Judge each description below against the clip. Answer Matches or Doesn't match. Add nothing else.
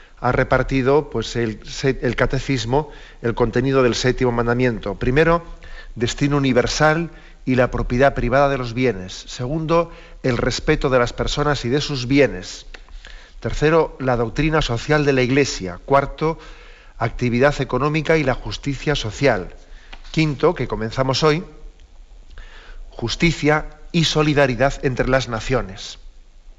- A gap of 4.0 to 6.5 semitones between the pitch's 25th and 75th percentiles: Doesn't match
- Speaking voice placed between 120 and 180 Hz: Matches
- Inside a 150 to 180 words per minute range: Doesn't match